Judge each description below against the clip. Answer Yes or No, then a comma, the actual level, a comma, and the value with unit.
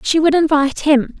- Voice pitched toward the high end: Yes, very high, 300 Hz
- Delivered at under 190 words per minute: No, average, 200 wpm